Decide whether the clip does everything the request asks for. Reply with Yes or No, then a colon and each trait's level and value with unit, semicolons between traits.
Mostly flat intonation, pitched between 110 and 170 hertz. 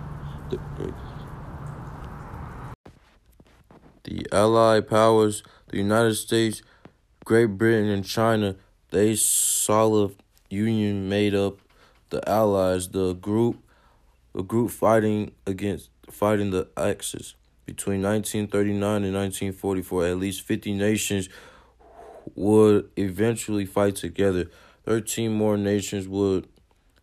No: narrow, 1.8 semitones; low, 100 Hz